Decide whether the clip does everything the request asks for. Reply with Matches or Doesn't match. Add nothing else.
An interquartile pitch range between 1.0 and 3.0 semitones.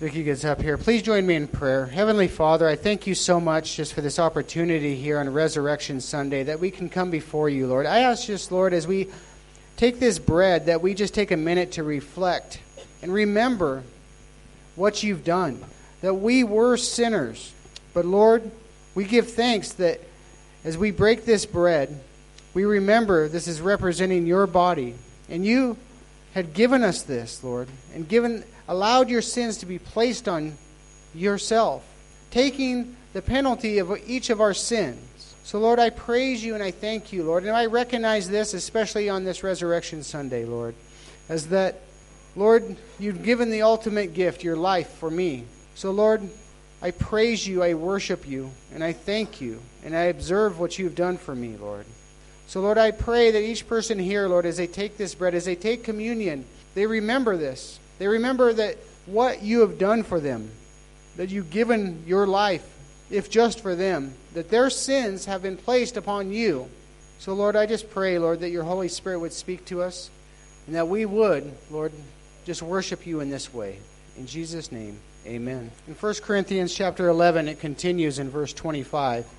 Doesn't match